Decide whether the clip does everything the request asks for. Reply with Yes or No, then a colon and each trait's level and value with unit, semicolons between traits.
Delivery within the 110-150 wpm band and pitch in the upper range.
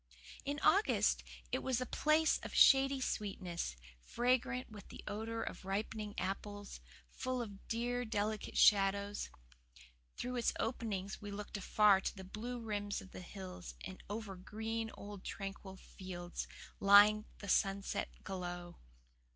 Yes: slow, 135 wpm; high, 205 Hz